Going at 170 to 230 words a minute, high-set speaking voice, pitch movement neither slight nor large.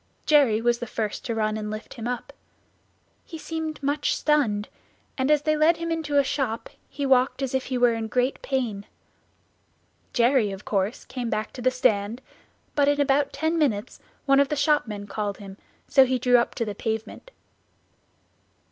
Yes: average, 185 wpm; very high, 250 Hz; average, 4.6 semitones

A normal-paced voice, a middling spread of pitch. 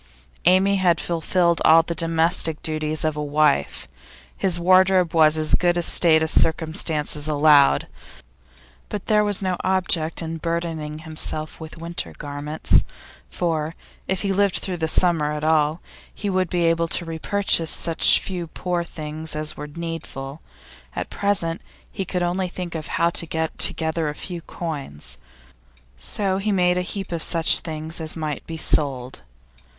No: average, 160 wpm; narrow, 2.3 semitones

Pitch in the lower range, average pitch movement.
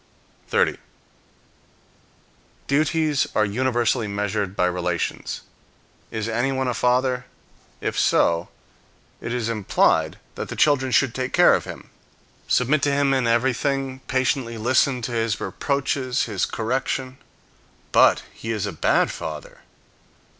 Yes: low, 125 Hz; average, 3.4 semitones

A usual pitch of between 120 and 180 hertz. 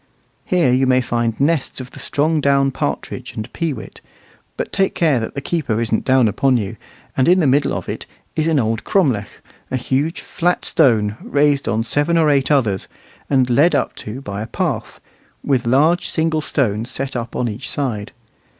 Yes: low, 135 Hz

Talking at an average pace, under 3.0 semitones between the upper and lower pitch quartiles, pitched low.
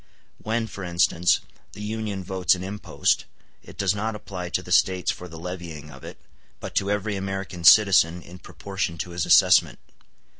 Yes: average, 175 wpm; narrow, 2.5 semitones; very low, 95 Hz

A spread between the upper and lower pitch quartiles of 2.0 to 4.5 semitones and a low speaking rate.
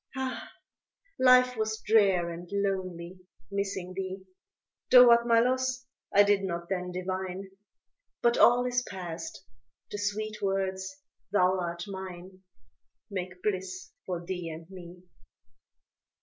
Yes: average, 3.1 semitones; slow, 120 wpm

